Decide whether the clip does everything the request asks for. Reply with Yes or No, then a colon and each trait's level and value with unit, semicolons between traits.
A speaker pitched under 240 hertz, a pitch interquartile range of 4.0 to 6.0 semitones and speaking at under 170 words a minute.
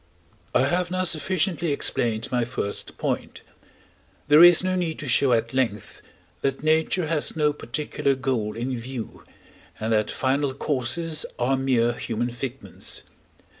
Yes: low, 135 Hz; average, 4.7 semitones; average, 140 wpm